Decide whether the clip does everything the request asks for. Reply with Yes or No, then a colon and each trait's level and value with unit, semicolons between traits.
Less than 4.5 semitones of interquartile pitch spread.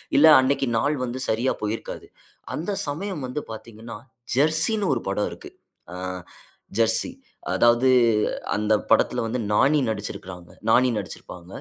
No: average, 4.8 semitones